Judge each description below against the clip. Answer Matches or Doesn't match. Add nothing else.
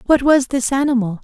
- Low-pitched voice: Doesn't match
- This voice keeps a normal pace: Matches